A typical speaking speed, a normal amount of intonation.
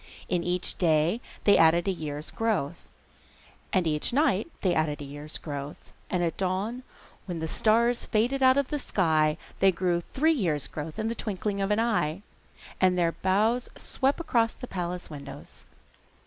No: average, 170 wpm; wide, 6.0 semitones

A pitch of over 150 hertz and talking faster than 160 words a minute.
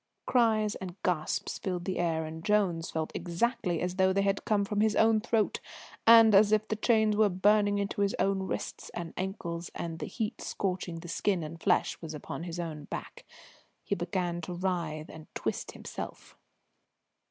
Yes: high, 190 Hz; average, 175 wpm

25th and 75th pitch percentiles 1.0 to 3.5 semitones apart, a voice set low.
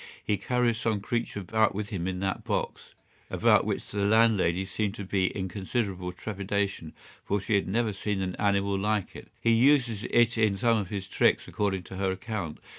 Yes: narrow, 2.5 semitones; low, 100 Hz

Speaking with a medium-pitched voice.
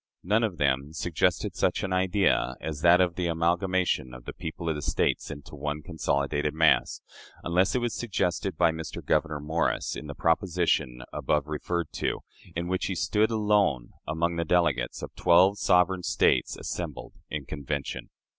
No: very low, 85 Hz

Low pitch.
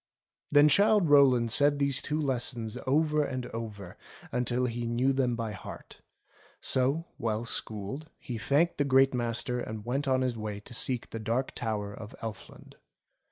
Yes: low, 125 Hz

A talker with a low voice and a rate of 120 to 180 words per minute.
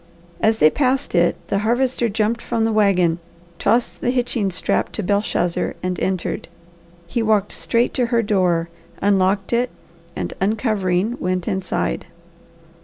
No: high, 205 Hz; average, 140 wpm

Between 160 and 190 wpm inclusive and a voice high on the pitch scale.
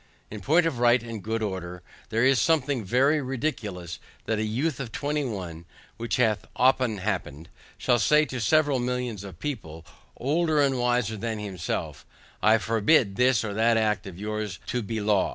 No: average, 175 wpm; low, 115 Hz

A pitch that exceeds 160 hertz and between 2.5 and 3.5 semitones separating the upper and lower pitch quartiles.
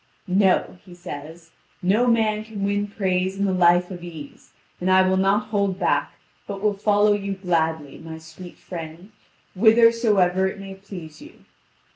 Yes: high, 190 Hz; average, 2.8 semitones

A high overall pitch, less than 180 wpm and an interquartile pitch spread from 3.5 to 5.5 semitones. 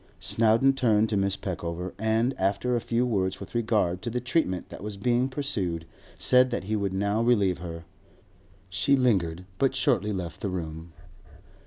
No: low, 105 Hz; average, 170 wpm; average, 4.7 semitones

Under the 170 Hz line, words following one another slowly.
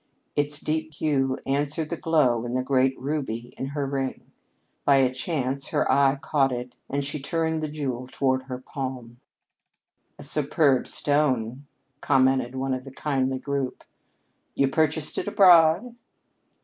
No: low, 135 Hz; average, 150 wpm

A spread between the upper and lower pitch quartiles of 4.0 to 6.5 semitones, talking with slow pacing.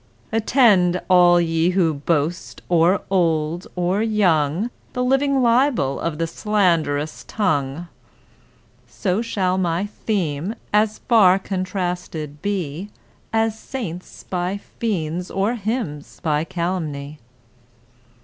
Yes: average, 4.4 semitones; slow, 105 wpm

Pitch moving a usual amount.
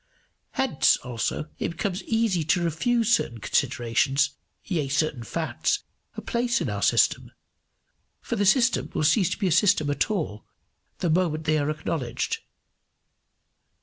No: wide, 6.5 semitones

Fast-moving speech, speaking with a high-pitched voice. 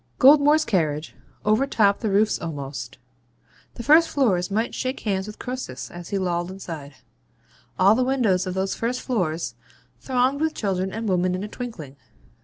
No: average, 160 wpm; high, 200 Hz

